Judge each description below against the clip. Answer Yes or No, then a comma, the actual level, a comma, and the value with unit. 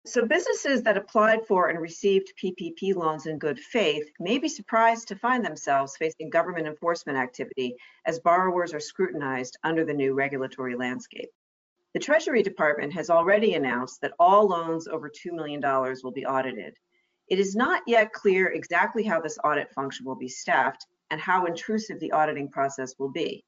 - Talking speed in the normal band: Yes, average, 170 wpm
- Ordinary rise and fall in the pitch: No, wide, 6.5 semitones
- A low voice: No, medium, 165 Hz